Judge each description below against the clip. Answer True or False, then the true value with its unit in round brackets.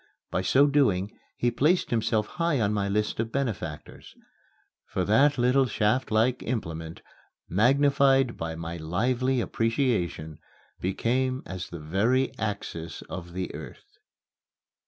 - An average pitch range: False (6.0 semitones)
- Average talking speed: False (120 wpm)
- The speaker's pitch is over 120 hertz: False (110 Hz)